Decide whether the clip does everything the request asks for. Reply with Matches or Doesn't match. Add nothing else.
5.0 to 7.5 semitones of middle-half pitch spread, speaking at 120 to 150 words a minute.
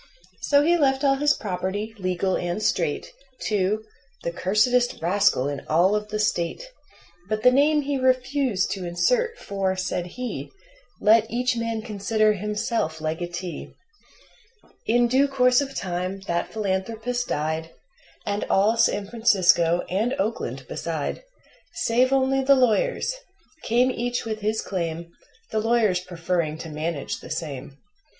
Matches